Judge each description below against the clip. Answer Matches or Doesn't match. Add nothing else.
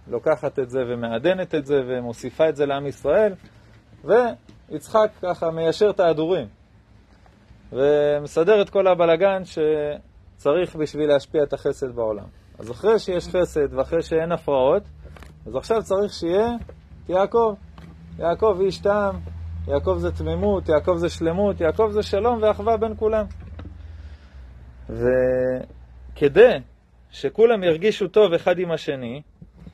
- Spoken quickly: Doesn't match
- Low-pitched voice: Doesn't match